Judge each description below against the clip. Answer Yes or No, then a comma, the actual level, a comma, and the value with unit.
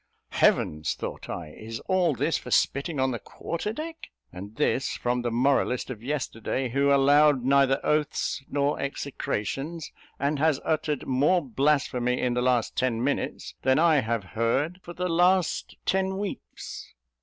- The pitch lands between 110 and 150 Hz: Yes, medium, 140 Hz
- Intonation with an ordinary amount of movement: Yes, average, 4.1 semitones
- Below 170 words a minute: Yes, average, 155 wpm